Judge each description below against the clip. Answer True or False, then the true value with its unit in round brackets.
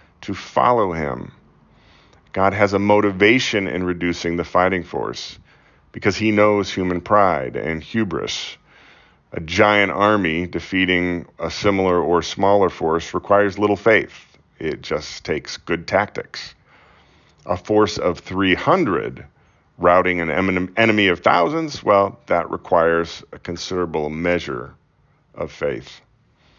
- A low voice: True (95 Hz)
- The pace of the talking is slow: True (120 wpm)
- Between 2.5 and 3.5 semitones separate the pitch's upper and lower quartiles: True (2.9 semitones)